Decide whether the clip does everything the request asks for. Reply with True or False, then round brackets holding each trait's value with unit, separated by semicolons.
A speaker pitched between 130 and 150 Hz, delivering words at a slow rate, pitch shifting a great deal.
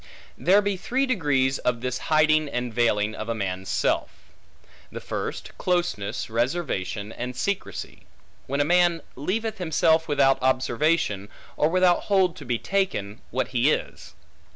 False (140 Hz; 145 wpm; 6.7 semitones)